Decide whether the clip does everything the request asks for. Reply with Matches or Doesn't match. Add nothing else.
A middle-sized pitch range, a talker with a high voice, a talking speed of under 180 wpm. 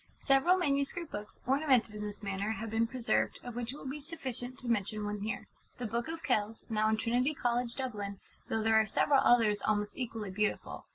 Doesn't match